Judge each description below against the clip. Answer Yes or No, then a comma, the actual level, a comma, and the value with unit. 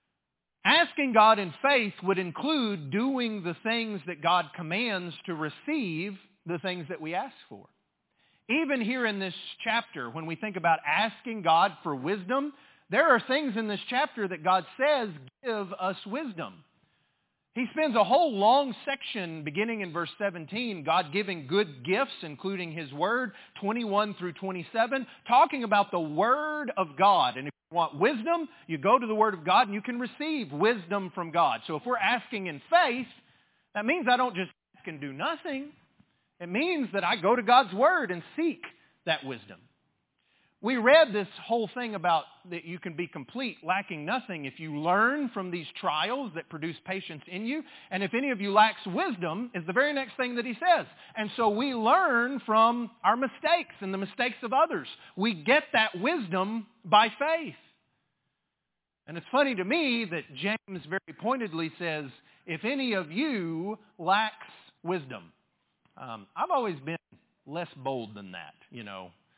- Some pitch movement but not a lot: No, wide, 6.2 semitones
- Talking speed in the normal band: Yes, average, 175 wpm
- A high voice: Yes, high, 210 Hz